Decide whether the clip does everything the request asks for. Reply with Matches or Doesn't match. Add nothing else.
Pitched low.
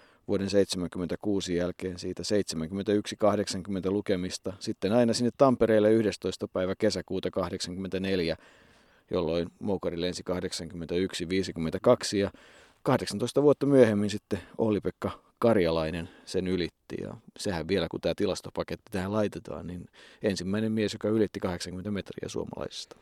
Matches